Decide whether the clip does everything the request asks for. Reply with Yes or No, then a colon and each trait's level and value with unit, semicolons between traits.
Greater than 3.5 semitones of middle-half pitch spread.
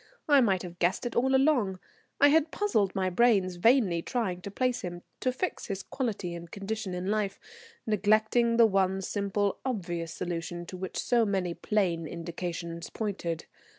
Yes: average, 4.7 semitones